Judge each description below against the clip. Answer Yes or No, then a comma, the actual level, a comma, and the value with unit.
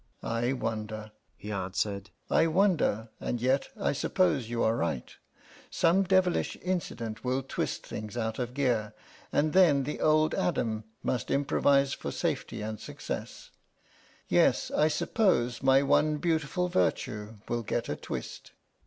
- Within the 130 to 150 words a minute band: Yes, average, 140 wpm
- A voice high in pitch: No, low, 125 Hz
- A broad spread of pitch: Yes, wide, 5.9 semitones